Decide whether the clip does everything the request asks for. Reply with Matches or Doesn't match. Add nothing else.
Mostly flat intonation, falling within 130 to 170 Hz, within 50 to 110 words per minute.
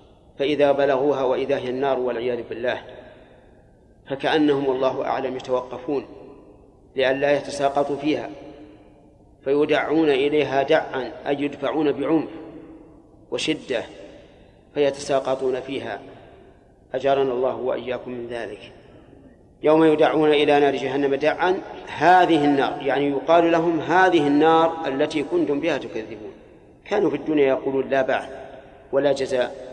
Matches